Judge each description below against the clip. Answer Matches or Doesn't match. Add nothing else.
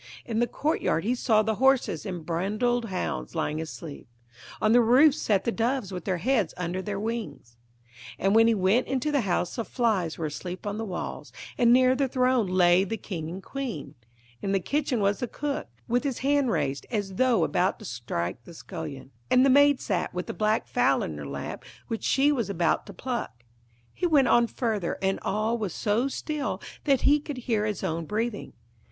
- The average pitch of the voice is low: Doesn't match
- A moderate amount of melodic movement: Doesn't match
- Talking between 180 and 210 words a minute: Matches